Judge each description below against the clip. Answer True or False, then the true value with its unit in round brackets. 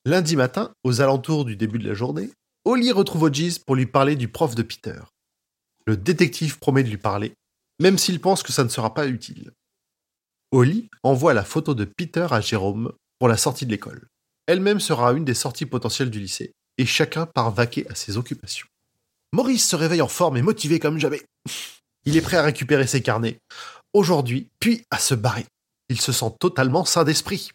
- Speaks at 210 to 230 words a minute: False (195 wpm)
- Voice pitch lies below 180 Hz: True (135 Hz)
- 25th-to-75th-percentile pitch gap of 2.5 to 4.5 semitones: False (5.4 semitones)